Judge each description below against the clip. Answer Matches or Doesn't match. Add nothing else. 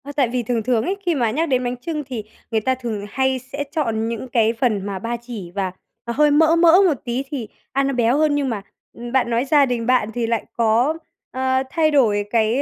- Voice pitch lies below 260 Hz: Matches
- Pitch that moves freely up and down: Doesn't match